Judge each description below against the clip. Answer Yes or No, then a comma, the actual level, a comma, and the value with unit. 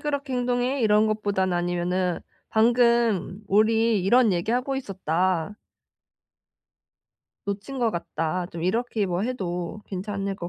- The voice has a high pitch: Yes, high, 205 Hz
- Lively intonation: No, average, 4.7 semitones